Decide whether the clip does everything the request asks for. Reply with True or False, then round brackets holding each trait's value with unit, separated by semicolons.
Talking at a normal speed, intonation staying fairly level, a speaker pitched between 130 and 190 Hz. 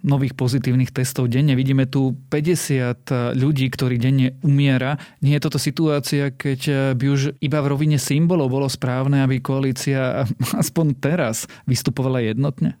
True (140 wpm; 2.0 semitones; 135 Hz)